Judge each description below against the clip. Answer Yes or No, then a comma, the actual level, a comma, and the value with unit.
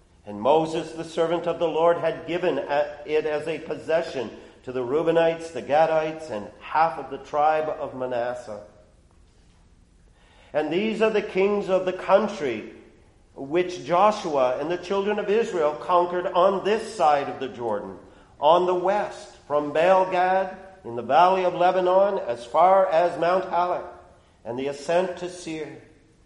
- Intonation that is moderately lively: No, wide, 5.9 semitones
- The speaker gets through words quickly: No, average, 155 wpm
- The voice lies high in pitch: No, medium, 160 Hz